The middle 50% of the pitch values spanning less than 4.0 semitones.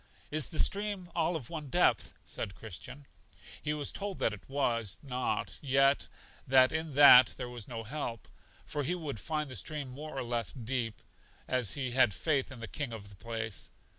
No: average, 4.5 semitones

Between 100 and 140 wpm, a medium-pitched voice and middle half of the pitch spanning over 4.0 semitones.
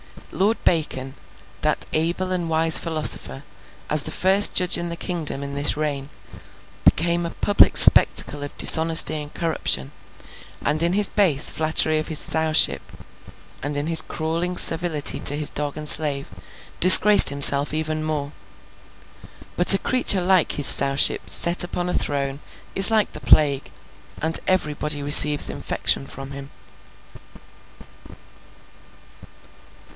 No: slow, 135 wpm; medium, 155 Hz; average, 3.1 semitones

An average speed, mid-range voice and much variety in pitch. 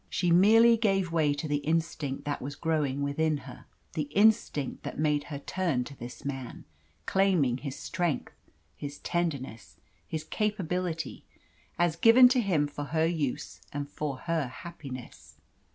No: average, 150 wpm; medium, 155 Hz; average, 3.8 semitones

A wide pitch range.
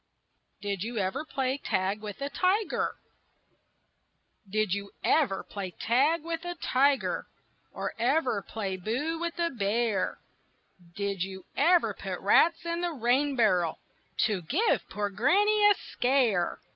Yes: wide, 8.3 semitones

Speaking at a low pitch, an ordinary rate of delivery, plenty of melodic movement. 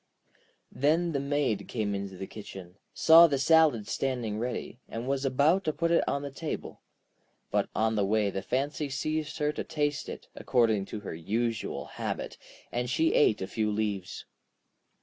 Yes: low, 125 Hz; average, 170 wpm; wide, 5.8 semitones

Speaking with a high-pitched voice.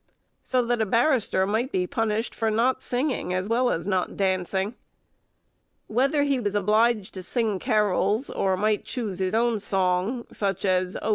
Yes: high, 215 Hz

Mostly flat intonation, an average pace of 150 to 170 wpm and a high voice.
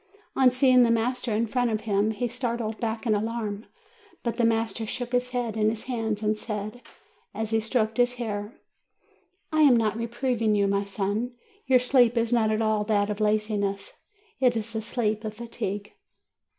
No: narrow, 2.2 semitones; average, 185 wpm; high, 225 Hz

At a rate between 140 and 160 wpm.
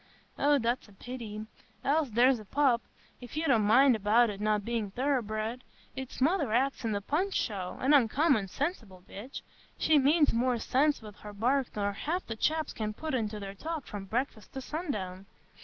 No: average, 175 wpm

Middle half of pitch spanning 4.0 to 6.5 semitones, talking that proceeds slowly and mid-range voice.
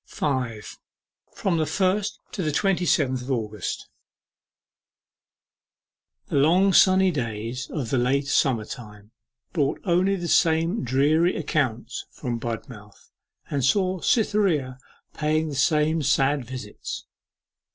Yes: wide, 5.6 semitones; slow, 120 wpm; medium, 145 Hz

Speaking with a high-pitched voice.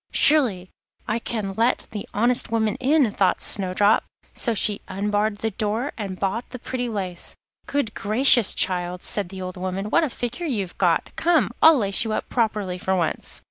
Yes: high, 210 Hz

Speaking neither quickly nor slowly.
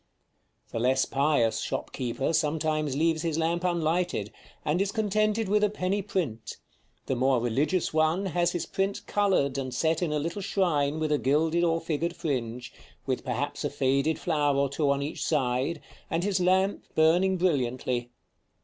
Yes: average, 165 wpm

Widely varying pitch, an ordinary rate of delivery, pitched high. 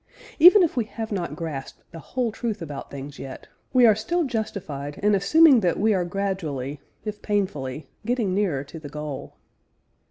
Yes: wide, 7.0 semitones; average, 170 wpm; high, 195 Hz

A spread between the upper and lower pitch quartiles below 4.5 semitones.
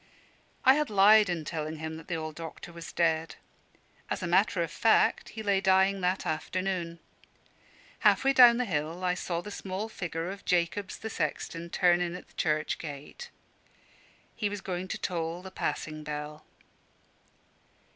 Yes: average, 3.2 semitones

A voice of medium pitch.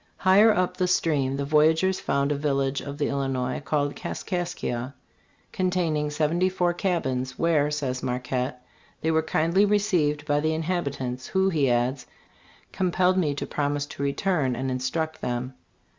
Yes: medium, 150 Hz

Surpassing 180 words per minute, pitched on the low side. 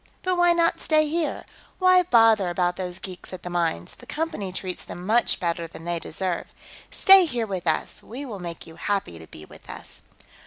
No: average, 200 wpm; high, 190 Hz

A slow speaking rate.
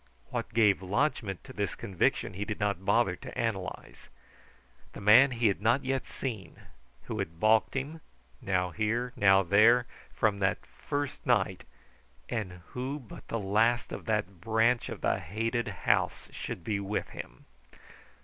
No: average, 155 wpm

